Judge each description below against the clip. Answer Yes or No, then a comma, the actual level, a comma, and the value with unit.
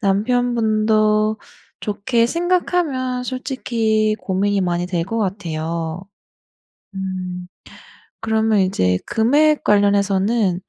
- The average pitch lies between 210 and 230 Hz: Yes, high, 215 Hz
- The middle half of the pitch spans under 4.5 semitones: Yes, average, 3.8 semitones